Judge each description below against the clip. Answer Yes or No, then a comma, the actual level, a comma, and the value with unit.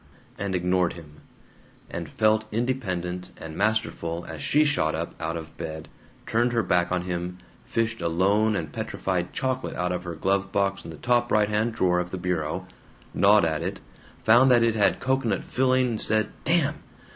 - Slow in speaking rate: No, average, 180 wpm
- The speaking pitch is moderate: No, low, 100 Hz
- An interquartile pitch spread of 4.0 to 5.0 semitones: Yes, average, 4.5 semitones